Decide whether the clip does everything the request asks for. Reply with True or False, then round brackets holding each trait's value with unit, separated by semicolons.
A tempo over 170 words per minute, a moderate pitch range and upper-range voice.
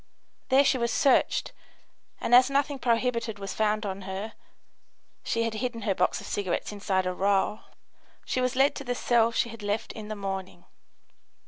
True (180 wpm; 3.8 semitones; 225 Hz)